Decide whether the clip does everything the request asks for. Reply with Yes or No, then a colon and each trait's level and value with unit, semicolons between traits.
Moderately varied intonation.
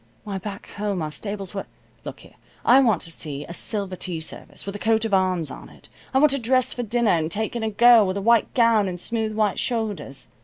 Yes: average, 3.6 semitones